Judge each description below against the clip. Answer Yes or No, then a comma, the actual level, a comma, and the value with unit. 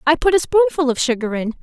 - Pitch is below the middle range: No, very high, 290 Hz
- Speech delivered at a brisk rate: Yes, fast, 260 wpm